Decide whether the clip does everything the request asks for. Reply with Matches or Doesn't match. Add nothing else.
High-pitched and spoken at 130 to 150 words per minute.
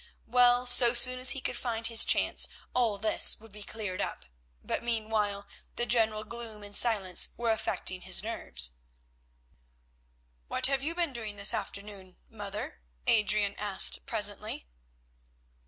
Matches